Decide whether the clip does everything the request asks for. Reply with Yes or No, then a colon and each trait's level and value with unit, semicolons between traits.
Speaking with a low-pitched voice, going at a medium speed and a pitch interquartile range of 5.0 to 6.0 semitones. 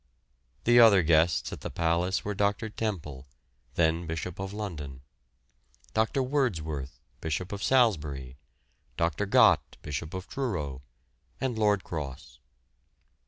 No: very low, 90 Hz; slow, 115 wpm; wide, 5.5 semitones